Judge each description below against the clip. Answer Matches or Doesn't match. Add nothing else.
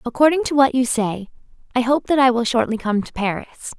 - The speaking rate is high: Matches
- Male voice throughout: Doesn't match